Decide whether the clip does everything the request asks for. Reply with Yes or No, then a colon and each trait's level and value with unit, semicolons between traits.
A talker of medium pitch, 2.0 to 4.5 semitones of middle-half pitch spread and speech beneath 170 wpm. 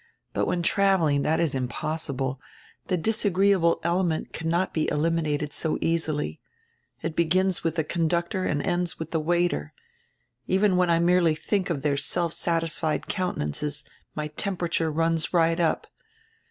Yes: medium, 165 Hz; narrow, 2.4 semitones; average, 155 wpm